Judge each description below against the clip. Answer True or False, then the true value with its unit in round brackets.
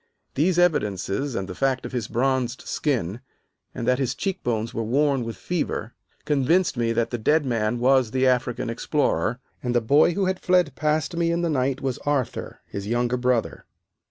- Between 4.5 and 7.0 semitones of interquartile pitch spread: False (4.0 semitones)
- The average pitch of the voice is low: True (130 Hz)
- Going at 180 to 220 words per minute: True (185 wpm)